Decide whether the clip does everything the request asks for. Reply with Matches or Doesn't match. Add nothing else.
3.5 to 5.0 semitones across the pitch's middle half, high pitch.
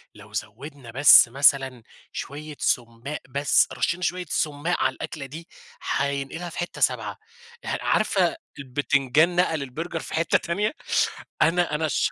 Doesn't match